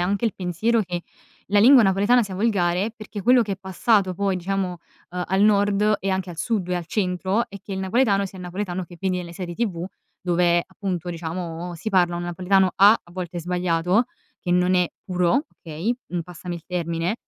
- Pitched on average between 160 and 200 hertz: Yes, medium, 185 Hz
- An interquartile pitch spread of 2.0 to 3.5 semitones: Yes, narrow, 2.5 semitones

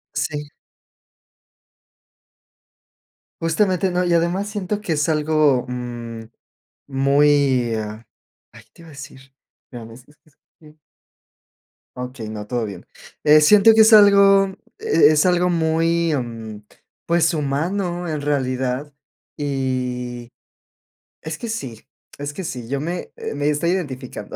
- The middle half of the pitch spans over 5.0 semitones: Yes, wide, 5.4 semitones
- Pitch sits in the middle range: Yes, medium, 150 Hz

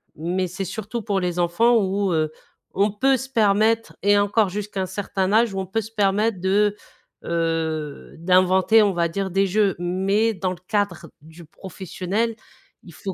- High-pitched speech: Yes, high, 195 Hz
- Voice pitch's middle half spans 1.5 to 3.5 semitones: Yes, average, 2.7 semitones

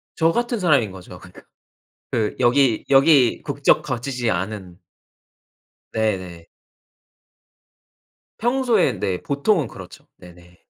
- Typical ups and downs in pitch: No, wide, 8.1 semitones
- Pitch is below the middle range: Yes, low, 120 Hz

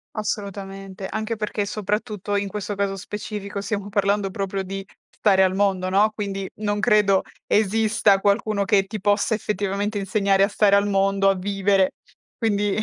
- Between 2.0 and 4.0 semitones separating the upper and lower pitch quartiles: No, narrow, 1.2 semitones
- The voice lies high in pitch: Yes, high, 200 Hz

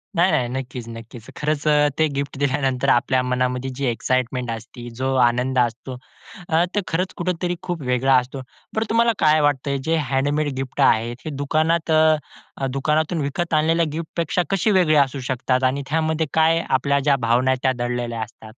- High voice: No, medium, 140 Hz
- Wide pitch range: No, average, 3.8 semitones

